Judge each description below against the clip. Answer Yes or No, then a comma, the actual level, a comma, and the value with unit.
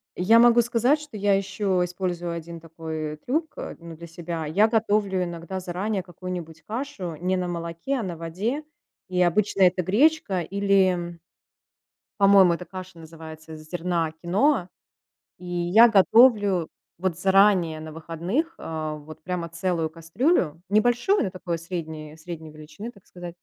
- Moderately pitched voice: Yes, medium, 180 Hz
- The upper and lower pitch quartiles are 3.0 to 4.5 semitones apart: Yes, average, 3.5 semitones